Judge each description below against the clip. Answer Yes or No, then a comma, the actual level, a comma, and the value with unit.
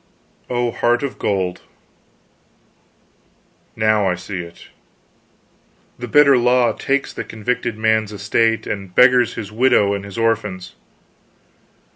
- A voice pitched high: No, low, 110 Hz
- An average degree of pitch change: Yes, average, 3.4 semitones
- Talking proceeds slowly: Yes, slow, 115 wpm